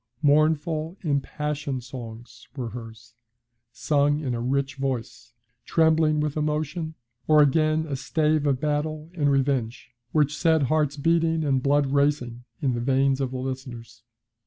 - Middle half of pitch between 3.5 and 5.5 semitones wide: No, average, 2.9 semitones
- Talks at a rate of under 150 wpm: Yes, average, 140 wpm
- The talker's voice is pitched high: No, medium, 145 Hz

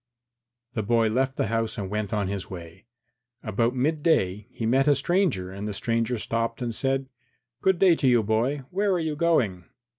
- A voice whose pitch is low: Yes, low, 115 Hz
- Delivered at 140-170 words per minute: No, average, 200 wpm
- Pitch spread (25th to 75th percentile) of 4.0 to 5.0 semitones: Yes, average, 4.7 semitones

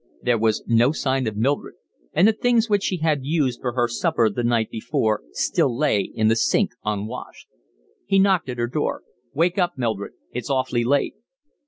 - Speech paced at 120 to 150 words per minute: No, average, 185 wpm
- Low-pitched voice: Yes, low, 125 Hz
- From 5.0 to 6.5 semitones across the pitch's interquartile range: Yes, wide, 5.4 semitones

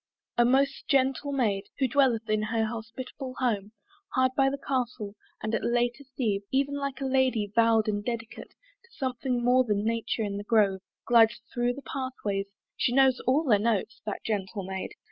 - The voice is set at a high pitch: Yes, high, 240 Hz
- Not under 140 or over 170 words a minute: No, average, 180 wpm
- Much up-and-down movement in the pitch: No, average, 3.6 semitones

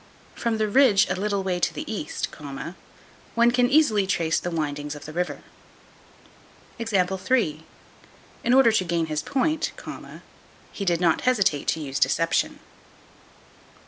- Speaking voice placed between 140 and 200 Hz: Yes, high, 190 Hz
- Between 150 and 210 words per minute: No, slow, 135 wpm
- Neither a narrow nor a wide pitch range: No, wide, 6.0 semitones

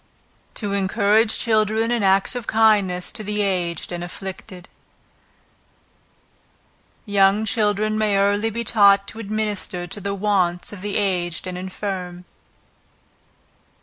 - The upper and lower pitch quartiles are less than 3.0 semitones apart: Yes, narrow, 2.5 semitones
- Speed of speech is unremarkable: No, slow, 120 wpm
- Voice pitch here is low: No, high, 200 Hz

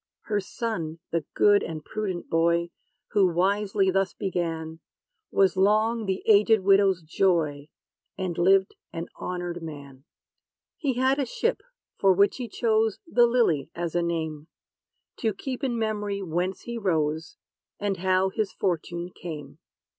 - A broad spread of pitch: No, average, 3.8 semitones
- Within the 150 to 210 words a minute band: No, average, 140 wpm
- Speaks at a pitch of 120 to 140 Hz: No, high, 190 Hz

